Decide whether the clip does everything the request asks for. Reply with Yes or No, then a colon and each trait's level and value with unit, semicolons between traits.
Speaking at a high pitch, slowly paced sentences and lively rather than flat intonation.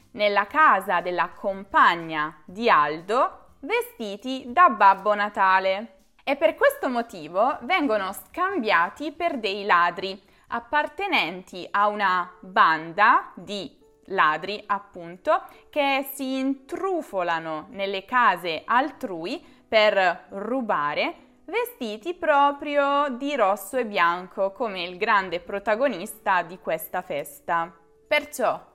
Yes: high, 210 Hz; slow, 100 wpm; wide, 7.4 semitones